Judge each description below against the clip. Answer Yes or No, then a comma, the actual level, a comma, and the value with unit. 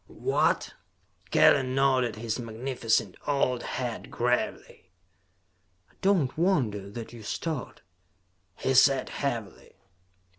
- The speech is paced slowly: Yes, slow, 105 wpm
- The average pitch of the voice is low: Yes, low, 125 Hz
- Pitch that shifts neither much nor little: Yes, average, 3.1 semitones